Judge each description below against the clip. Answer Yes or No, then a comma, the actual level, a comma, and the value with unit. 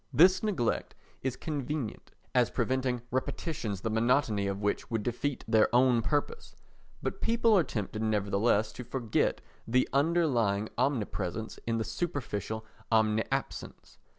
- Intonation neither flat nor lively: Yes, average, 4.7 semitones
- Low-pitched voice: Yes, low, 120 Hz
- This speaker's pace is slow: Yes, slow, 125 wpm